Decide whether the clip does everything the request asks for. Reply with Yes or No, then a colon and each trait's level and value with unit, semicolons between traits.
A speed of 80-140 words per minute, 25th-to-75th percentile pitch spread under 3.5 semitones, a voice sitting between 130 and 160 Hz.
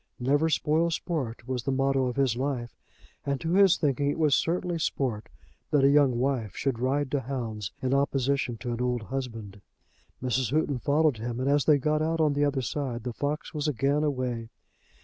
No: average, 195 wpm; average, 3.0 semitones; low, 135 Hz